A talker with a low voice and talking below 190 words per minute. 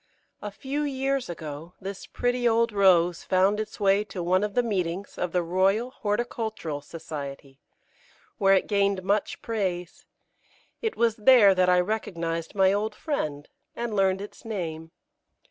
No: high, 195 Hz; average, 150 wpm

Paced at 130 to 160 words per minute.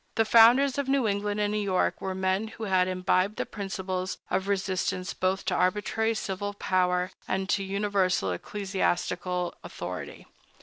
Yes: average, 150 wpm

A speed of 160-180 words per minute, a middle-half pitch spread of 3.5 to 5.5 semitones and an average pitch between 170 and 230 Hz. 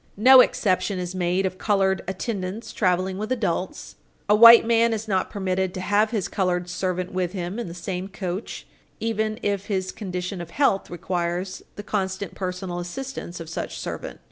No: average, 170 wpm; narrow, 2.6 semitones; high, 190 Hz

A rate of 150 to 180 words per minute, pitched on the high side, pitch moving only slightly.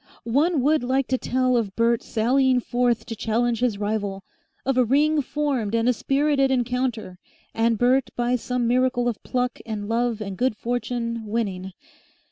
Yes: average, 165 wpm; high, 245 Hz; narrow, 2.3 semitones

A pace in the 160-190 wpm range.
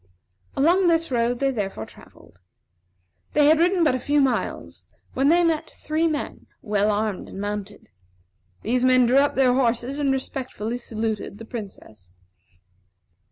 No: average, 150 wpm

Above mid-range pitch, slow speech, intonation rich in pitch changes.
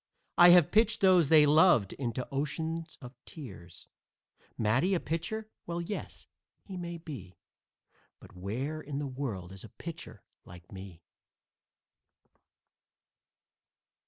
No: medium, 145 Hz; slow, 120 wpm; wide, 8.2 semitones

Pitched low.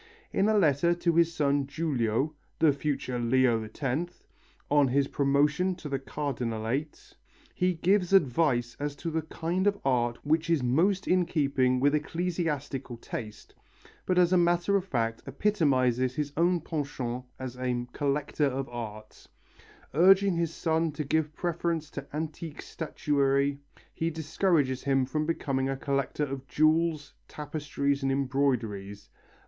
No: medium, 145 Hz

